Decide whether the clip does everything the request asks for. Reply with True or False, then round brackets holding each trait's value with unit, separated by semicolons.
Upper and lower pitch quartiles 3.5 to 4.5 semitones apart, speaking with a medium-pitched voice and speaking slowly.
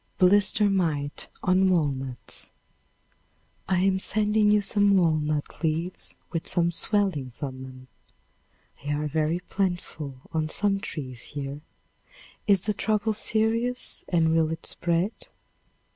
False (5.2 semitones; 170 Hz; 120 wpm)